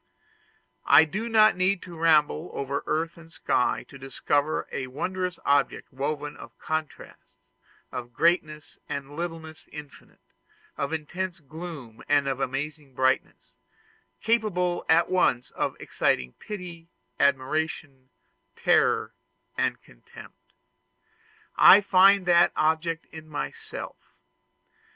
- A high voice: No, medium, 155 Hz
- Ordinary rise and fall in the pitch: Yes, average, 3.8 semitones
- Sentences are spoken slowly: Yes, slow, 105 wpm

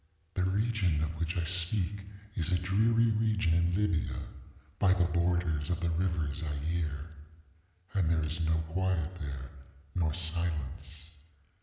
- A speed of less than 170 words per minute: Yes, average, 140 wpm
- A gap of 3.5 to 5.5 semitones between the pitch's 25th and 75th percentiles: No, average, 2.8 semitones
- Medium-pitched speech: No, very low, 85 Hz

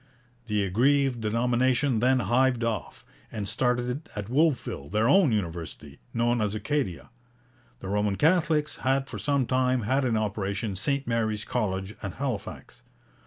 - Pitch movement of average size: Yes, average, 4.1 semitones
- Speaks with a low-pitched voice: Yes, low, 120 Hz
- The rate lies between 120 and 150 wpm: Yes, average, 140 wpm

